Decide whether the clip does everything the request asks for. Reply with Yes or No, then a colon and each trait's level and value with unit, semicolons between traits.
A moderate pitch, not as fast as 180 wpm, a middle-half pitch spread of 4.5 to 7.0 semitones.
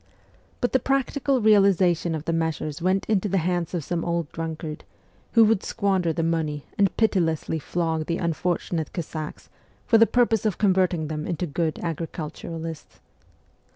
No: medium, 170 Hz; average, 155 wpm; average, 3.5 semitones